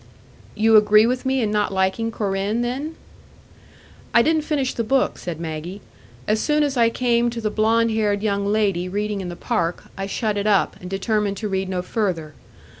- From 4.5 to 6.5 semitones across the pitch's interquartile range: No, average, 3.2 semitones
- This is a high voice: Yes, high, 210 Hz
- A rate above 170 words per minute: Yes, average, 190 wpm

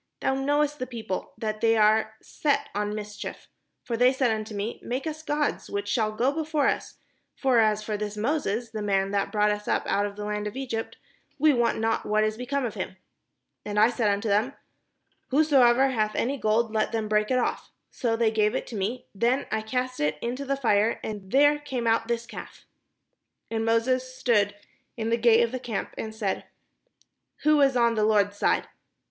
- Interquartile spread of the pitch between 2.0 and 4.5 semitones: Yes, average, 3.3 semitones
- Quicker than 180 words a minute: Yes, fast, 205 wpm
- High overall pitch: Yes, high, 225 Hz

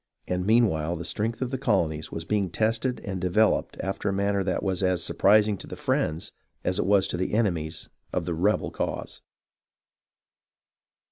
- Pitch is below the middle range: Yes, very low, 95 Hz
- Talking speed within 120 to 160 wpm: No, average, 185 wpm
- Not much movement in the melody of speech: No, average, 3.5 semitones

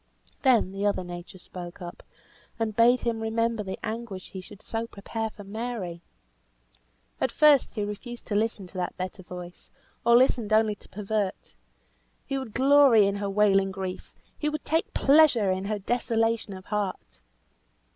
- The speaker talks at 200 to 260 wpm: No, average, 165 wpm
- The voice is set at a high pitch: Yes, high, 215 Hz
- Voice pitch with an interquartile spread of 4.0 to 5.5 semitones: No, average, 3.3 semitones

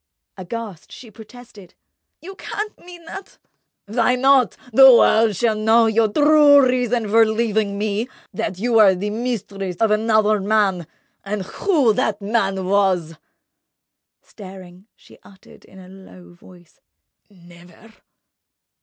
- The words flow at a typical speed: No, slow, 120 wpm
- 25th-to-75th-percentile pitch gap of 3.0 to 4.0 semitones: Yes, average, 3.6 semitones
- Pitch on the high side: Yes, high, 215 Hz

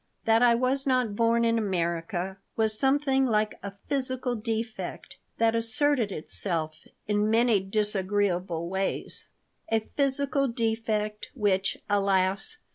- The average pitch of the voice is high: Yes, high, 220 Hz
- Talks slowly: Yes, slow, 120 wpm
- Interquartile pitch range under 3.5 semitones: No, average, 3.9 semitones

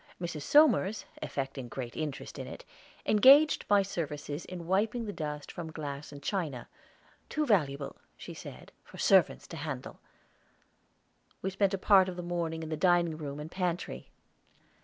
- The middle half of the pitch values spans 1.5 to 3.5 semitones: No, average, 4.7 semitones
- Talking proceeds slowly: No, average, 160 wpm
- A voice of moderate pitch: Yes, medium, 170 Hz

